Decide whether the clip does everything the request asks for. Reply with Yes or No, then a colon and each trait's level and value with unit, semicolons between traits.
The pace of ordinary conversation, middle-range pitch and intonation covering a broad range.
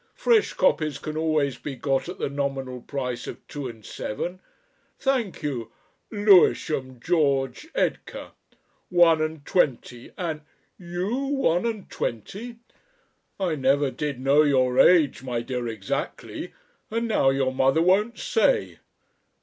No: slow, 130 wpm; medium, 150 Hz; wide, 5.8 semitones